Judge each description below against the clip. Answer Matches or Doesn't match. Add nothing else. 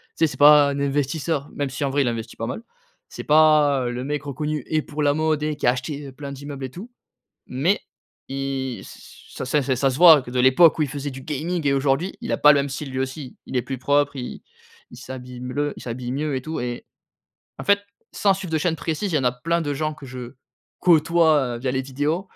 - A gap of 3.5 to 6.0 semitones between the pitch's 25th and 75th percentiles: Doesn't match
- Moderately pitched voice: Matches